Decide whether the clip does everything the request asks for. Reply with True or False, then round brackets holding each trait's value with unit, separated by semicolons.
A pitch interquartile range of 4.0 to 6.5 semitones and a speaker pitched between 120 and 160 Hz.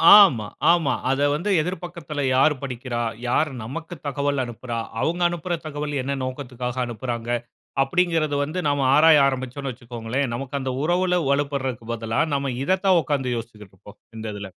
True (4.3 semitones; 140 Hz)